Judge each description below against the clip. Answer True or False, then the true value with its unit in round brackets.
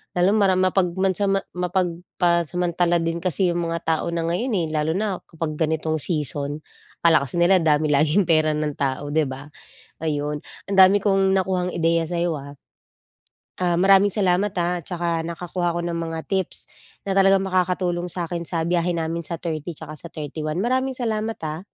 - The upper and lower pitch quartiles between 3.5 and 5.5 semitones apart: False (2.8 semitones)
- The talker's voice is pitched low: False (170 Hz)